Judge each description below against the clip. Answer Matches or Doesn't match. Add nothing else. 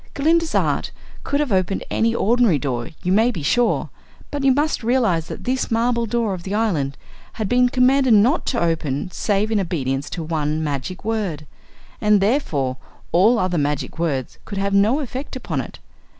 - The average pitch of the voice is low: Doesn't match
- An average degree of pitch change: Doesn't match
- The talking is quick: Doesn't match